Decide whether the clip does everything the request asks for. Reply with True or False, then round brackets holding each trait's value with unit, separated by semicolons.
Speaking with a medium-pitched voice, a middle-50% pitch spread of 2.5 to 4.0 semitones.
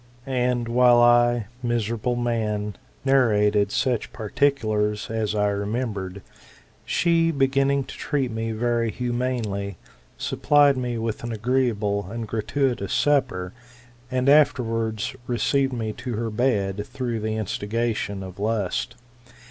False (115 Hz; 3.2 semitones)